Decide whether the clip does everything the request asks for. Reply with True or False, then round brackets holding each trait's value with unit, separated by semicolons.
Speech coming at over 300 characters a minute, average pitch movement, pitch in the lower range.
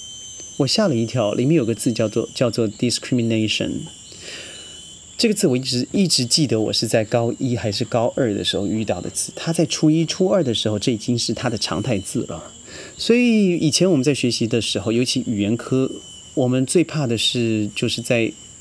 True (320 characters per minute; 4.6 semitones; 120 Hz)